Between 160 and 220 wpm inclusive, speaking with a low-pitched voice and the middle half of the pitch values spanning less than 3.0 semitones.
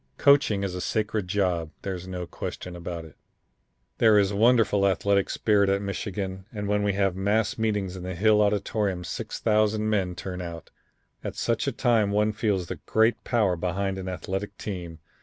Yes: average, 175 wpm; low, 100 Hz; narrow, 2.5 semitones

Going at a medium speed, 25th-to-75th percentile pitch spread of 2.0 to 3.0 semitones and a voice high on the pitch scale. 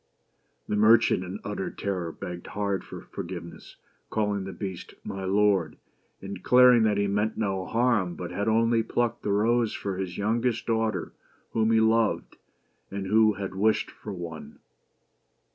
No: average, 160 wpm; average, 2.7 semitones; low, 105 Hz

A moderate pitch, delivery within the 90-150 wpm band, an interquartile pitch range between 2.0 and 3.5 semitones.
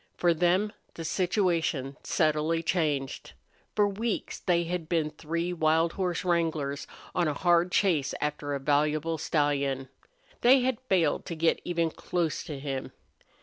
Yes: medium, 165 Hz; average, 145 wpm; average, 3.0 semitones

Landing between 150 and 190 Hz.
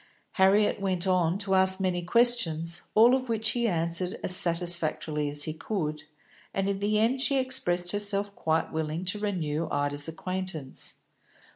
Yes: medium, 185 Hz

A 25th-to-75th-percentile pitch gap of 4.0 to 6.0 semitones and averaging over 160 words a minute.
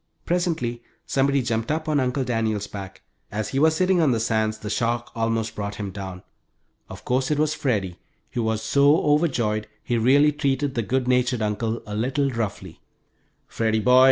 Yes: average, 4.3 semitones; average, 180 wpm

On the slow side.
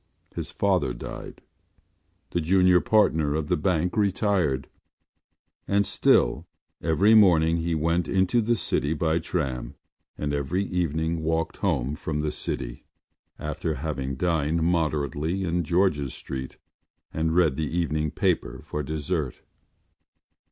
Yes: slow, 125 wpm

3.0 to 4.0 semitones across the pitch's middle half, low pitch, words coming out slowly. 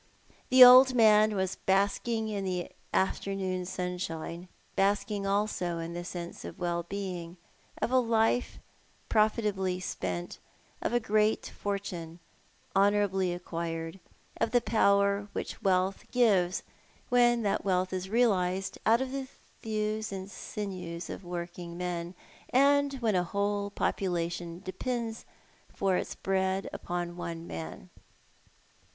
No: average, 3.4 semitones; high, 195 Hz; slow, 125 wpm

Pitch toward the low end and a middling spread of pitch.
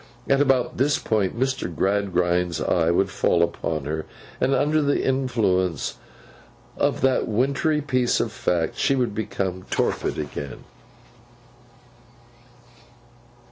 No: low, 105 Hz; wide, 7.2 semitones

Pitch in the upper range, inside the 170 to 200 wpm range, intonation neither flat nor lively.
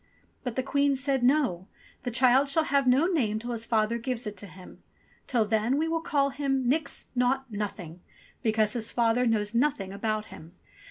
Yes: high, 245 Hz; average, 195 wpm; average, 4.2 semitones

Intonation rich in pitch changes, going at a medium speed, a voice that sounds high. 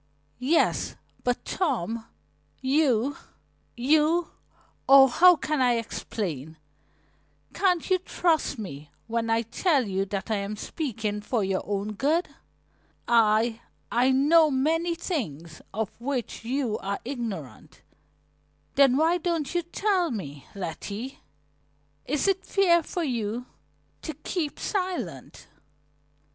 No: wide, 7.1 semitones; slow, 115 wpm; very high, 255 Hz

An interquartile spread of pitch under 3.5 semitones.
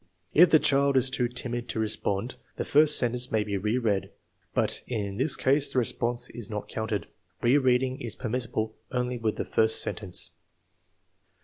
Yes: average, 2.9 semitones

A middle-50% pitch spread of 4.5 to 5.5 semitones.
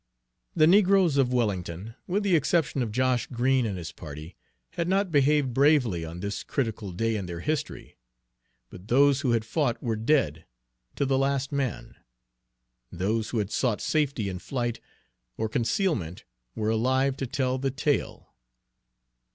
Yes: average, 5.0 semitones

